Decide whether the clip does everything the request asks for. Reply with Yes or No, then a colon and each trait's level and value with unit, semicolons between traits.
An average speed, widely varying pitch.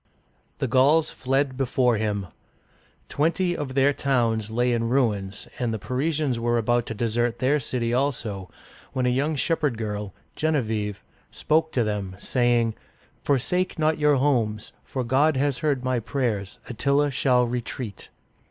No: average, 160 wpm; average, 3.8 semitones